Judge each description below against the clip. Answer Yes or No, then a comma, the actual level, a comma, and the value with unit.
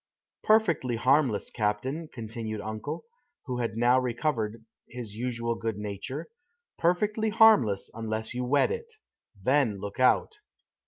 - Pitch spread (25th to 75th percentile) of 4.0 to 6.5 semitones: Yes, wide, 5.4 semitones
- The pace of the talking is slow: Yes, slow, 120 wpm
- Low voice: Yes, low, 120 Hz